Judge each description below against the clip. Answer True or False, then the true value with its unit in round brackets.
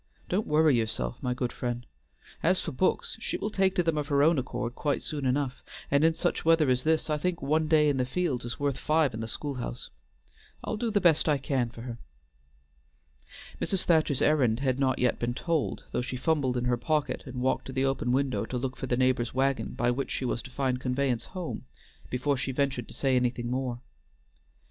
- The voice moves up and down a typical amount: True (3.7 semitones)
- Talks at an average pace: False (220 wpm)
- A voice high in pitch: False (135 Hz)